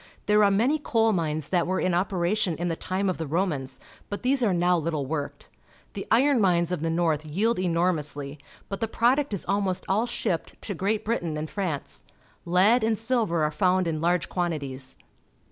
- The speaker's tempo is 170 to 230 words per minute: Yes, average, 190 wpm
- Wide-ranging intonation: No, average, 4.5 semitones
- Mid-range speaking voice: Yes, medium, 180 Hz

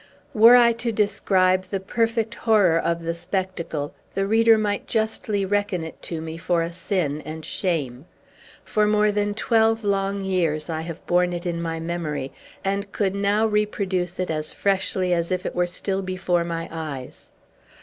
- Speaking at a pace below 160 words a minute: No, average, 170 wpm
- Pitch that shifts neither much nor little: Yes, average, 3.6 semitones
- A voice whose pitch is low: No, medium, 185 Hz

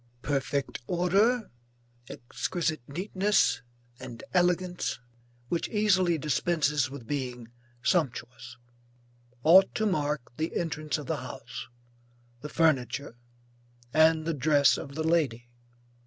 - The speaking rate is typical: No, slow, 105 wpm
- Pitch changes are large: No, average, 4.4 semitones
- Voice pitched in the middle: Yes, medium, 155 Hz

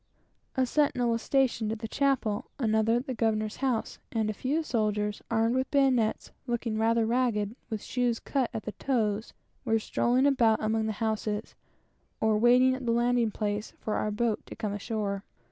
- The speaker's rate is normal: Yes, average, 180 wpm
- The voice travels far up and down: No, narrow, 2.5 semitones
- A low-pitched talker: No, high, 225 Hz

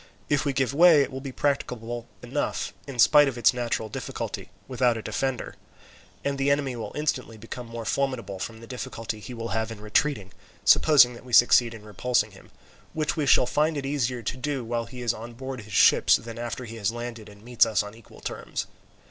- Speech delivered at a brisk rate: Yes, fast, 210 wpm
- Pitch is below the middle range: Yes, low, 120 Hz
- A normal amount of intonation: Yes, average, 3.1 semitones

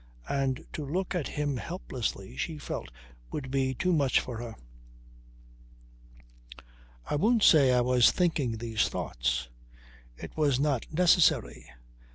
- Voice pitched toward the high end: No, low, 135 Hz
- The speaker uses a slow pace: Yes, slow, 130 wpm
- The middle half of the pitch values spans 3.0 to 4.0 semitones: No, average, 4.5 semitones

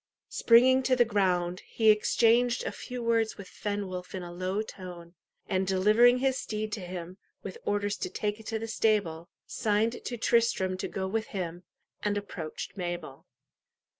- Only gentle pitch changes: No, average, 3.7 semitones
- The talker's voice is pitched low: No, high, 205 Hz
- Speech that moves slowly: No, average, 165 wpm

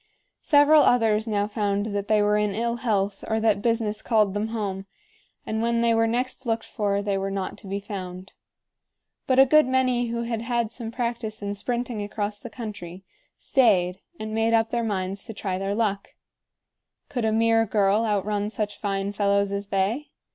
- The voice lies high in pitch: Yes, high, 215 Hz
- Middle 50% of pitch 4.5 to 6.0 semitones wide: No, narrow, 2.5 semitones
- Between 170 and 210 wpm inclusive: Yes, average, 185 wpm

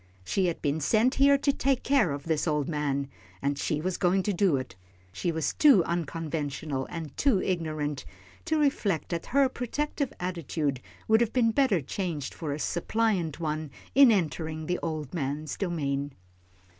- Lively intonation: Yes, wide, 6.5 semitones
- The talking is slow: No, average, 170 wpm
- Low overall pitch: No, medium, 165 Hz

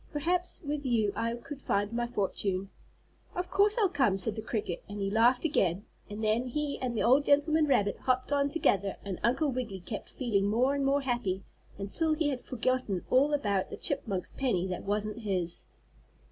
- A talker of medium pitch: No, high, 240 Hz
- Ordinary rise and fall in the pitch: No, wide, 5.8 semitones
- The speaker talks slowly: No, average, 190 wpm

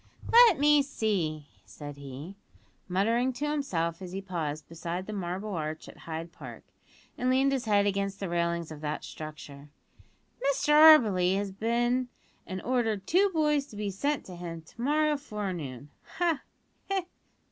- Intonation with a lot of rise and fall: Yes, wide, 8.2 semitones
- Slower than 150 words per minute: No, average, 160 wpm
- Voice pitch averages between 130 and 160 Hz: No, high, 200 Hz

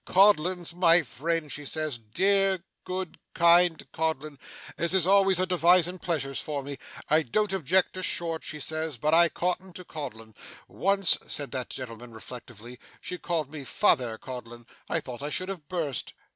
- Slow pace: No, average, 165 wpm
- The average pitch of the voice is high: No, medium, 160 Hz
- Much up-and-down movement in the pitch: No, average, 4.8 semitones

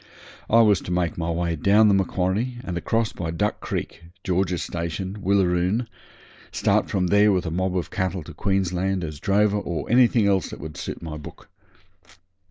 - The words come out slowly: No, average, 175 wpm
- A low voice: Yes, very low, 95 Hz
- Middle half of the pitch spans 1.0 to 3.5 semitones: Yes, average, 2.8 semitones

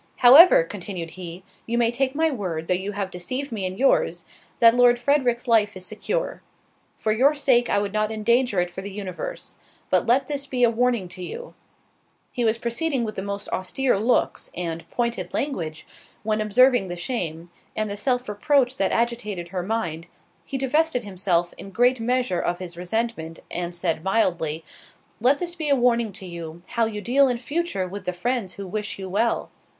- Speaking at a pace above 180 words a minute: Yes, average, 190 wpm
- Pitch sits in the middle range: No, high, 220 Hz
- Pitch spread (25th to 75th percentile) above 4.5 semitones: Yes, average, 5.2 semitones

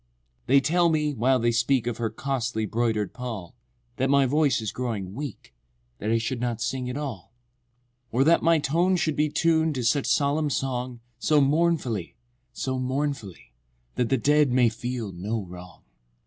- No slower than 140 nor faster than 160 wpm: No, average, 175 wpm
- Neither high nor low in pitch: No, low, 125 Hz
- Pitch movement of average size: Yes, average, 4.1 semitones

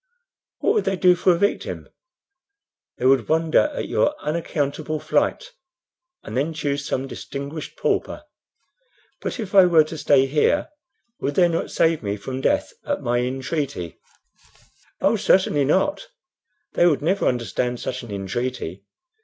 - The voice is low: No, medium, 150 Hz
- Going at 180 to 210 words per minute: No, average, 145 wpm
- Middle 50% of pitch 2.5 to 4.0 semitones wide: No, average, 5.2 semitones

